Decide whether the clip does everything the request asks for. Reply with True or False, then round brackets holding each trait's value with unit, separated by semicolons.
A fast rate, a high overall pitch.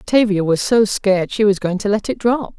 True (255 wpm; 205 Hz)